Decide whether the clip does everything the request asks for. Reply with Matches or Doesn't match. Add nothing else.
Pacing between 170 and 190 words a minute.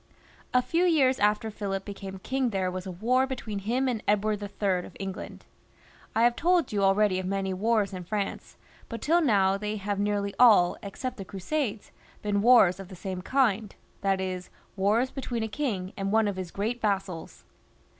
Matches